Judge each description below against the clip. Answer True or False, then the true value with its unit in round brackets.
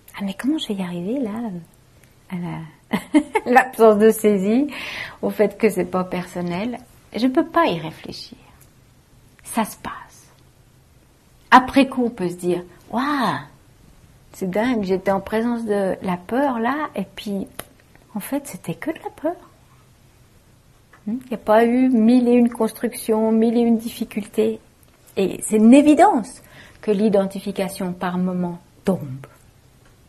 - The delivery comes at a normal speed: True (150 wpm)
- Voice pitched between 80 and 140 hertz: False (210 Hz)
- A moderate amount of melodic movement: True (5.0 semitones)